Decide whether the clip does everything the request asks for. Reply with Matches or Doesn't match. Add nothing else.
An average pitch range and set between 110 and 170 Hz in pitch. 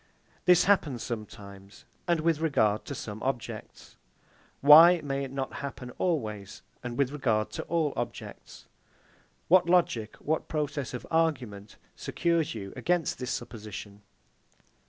Doesn't match